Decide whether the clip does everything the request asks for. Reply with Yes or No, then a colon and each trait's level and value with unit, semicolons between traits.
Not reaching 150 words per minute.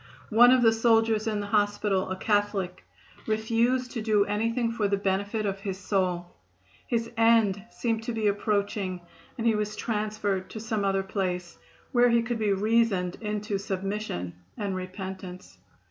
No: average, 160 wpm